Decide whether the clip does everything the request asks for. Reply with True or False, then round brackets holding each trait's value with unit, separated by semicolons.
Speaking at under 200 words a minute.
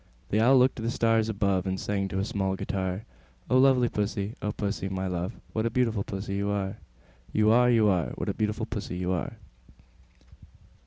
False (205 wpm)